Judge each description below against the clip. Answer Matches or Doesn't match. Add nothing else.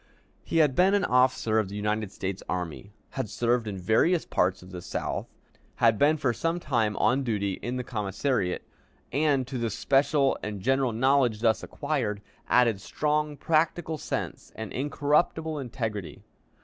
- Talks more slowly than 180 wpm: Matches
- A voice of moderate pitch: Doesn't match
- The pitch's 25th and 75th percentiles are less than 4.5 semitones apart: Doesn't match